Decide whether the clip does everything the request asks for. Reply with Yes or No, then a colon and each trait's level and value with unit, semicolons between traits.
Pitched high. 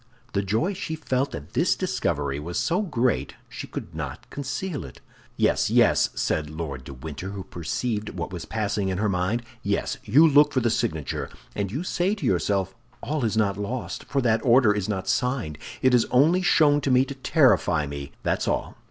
No: low, 110 Hz